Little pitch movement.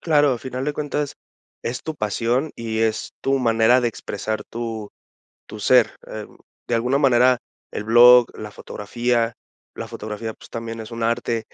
Yes: narrow, 2.3 semitones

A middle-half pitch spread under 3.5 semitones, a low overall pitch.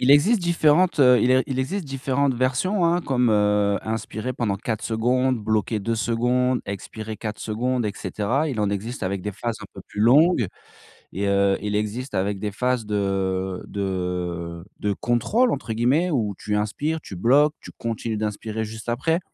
No: average, 4.1 semitones; low, 115 Hz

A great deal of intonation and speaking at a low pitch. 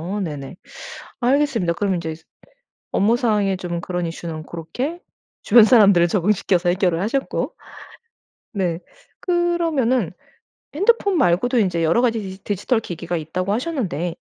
No: wide, 6.3 semitones; high, 195 Hz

